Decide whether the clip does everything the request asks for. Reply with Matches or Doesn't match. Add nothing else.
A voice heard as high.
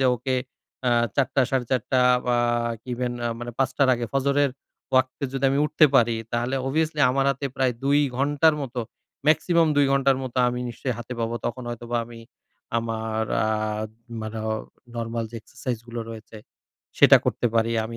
Doesn't match